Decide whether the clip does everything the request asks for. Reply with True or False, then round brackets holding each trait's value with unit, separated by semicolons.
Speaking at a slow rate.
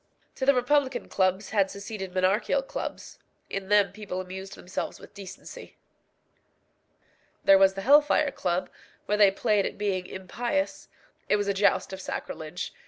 False (155 wpm)